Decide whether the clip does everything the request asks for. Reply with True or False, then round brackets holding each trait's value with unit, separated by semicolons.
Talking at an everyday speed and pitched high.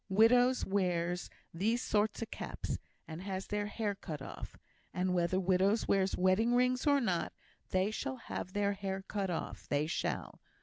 True (165 wpm; 195 Hz)